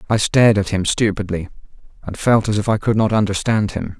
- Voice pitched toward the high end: No, low, 105 Hz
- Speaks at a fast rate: Yes, fast, 210 wpm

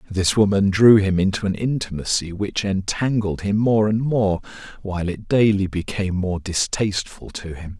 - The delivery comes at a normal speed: Yes, average, 160 wpm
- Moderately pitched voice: No, low, 100 Hz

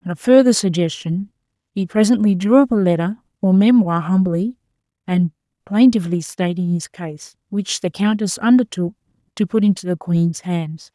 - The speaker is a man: No, female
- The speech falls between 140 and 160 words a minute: Yes, average, 155 wpm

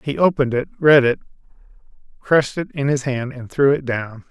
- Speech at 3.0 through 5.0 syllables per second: No, 5.5 syllables/s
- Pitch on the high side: No, low, 135 Hz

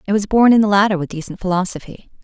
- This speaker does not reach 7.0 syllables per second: No, 7.5 syllables/s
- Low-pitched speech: No, high, 195 Hz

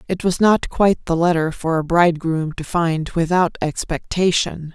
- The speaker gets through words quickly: No, average, 165 wpm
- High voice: No, medium, 170 Hz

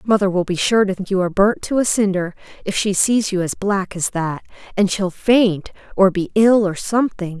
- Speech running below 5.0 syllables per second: No, 5.2 syllables/s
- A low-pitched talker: No, high, 195 Hz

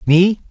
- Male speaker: Yes, male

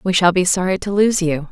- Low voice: No, medium, 185 Hz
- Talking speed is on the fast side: Yes, fast, 280 wpm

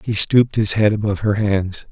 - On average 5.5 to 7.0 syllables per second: Yes, 5.6 syllables/s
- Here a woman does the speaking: No, male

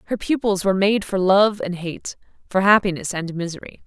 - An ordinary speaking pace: Yes, average, 185 wpm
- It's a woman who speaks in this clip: Yes, female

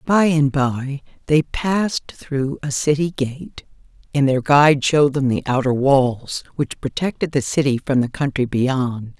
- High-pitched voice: No, medium, 140 Hz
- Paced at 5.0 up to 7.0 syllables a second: No, 4.2 syllables/s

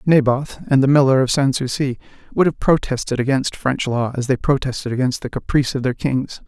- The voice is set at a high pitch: No, low, 135 Hz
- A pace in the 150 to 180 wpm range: No, fast, 205 wpm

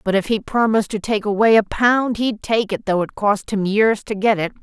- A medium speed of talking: No, fast, 260 wpm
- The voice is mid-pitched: No, high, 210 Hz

